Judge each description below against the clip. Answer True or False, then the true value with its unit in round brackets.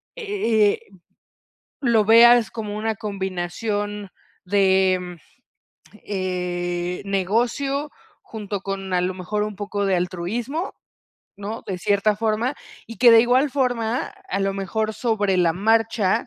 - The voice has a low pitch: False (205 Hz)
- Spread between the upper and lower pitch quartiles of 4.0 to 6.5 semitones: False (3.2 semitones)